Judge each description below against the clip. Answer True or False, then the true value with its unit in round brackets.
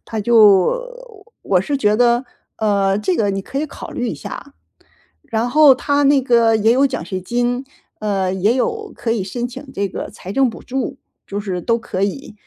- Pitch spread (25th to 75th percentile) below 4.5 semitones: False (4.9 semitones)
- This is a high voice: True (230 Hz)